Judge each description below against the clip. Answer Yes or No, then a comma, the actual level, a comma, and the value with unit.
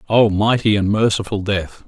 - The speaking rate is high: No, average, 160 wpm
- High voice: No, low, 105 Hz